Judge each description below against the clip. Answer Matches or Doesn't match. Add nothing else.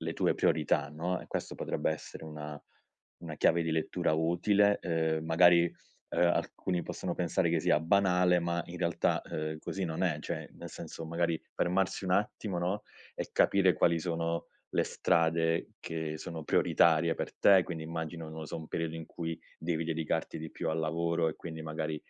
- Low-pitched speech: Matches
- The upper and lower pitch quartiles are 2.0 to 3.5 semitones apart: Doesn't match